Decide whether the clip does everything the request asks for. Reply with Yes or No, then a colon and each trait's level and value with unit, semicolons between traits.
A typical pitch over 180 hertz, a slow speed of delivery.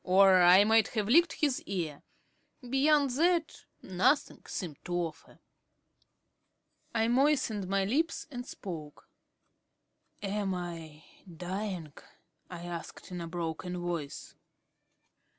Yes: high, 190 Hz; slow, 110 wpm